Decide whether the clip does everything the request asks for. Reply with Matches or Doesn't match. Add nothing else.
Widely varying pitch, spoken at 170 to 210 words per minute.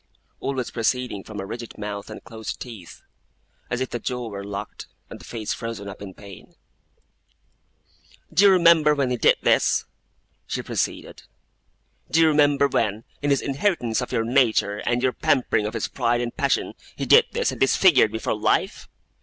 Doesn't match